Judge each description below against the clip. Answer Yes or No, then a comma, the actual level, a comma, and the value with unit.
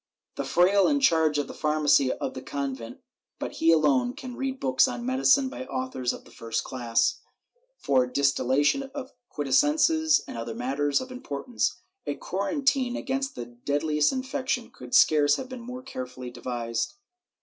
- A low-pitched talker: No, medium, 150 Hz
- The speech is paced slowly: No, average, 160 wpm